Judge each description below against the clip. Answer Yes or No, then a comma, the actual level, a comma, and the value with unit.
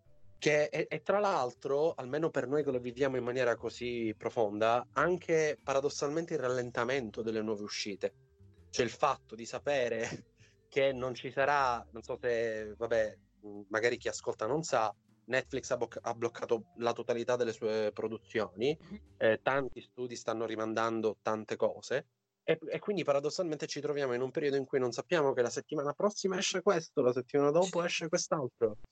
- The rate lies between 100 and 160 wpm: No, fast, 170 wpm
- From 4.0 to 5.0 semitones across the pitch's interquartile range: Yes, average, 4.7 semitones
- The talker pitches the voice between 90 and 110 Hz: No, low, 125 Hz